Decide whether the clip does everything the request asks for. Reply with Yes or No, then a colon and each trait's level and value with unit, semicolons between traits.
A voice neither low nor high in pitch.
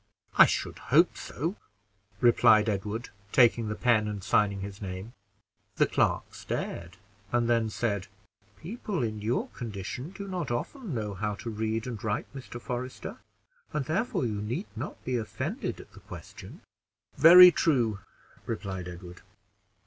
No: low, 115 Hz